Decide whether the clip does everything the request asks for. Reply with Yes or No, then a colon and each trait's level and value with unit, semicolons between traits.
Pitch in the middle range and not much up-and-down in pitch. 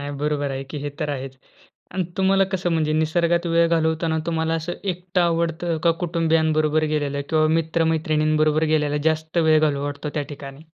Yes: medium, 160 Hz; narrow, 1.9 semitones